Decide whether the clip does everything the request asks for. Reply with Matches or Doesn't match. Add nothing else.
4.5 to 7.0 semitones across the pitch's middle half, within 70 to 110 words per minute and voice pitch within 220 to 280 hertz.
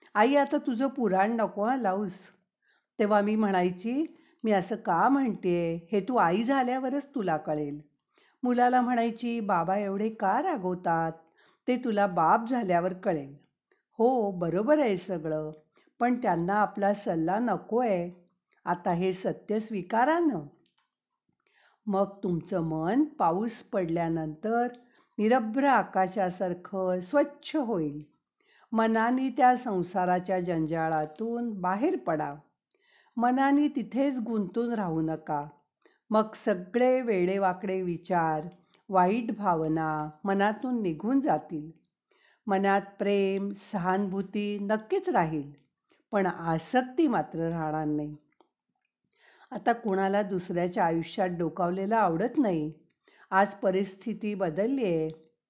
Doesn't match